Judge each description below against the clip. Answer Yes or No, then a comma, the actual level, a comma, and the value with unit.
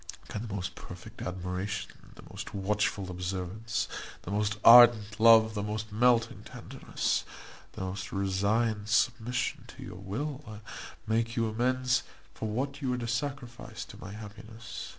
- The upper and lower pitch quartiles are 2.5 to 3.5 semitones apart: Yes, average, 2.8 semitones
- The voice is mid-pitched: No, low, 110 Hz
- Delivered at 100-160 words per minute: Yes, average, 145 wpm